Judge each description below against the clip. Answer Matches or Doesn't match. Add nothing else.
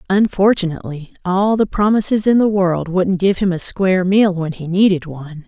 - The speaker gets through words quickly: Doesn't match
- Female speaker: Matches